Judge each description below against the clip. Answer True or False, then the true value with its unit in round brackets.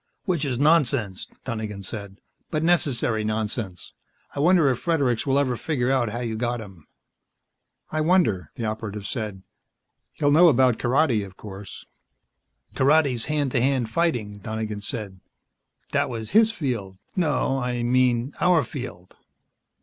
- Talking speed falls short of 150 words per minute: True (140 wpm)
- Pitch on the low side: True (120 Hz)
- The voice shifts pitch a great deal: False (4.9 semitones)